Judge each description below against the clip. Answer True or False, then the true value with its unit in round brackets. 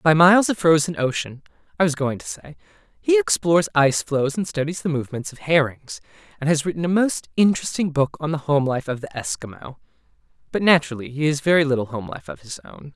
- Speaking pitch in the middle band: True (145 Hz)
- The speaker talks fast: True (210 wpm)